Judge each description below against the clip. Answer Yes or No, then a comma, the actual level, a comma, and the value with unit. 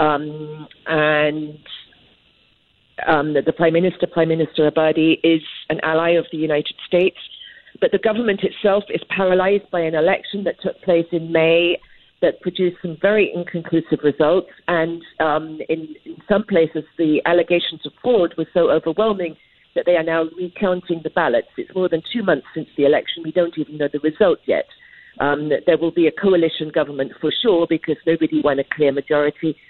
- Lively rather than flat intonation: No, narrow, 2.4 semitones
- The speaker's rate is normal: Yes, average, 175 wpm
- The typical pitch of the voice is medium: Yes, medium, 165 Hz